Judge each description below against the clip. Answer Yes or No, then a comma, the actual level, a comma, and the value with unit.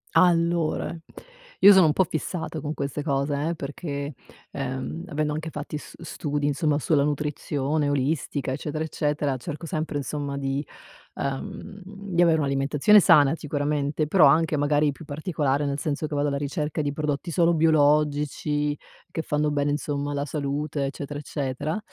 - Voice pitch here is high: No, medium, 150 Hz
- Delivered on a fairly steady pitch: Yes, narrow, 1.8 semitones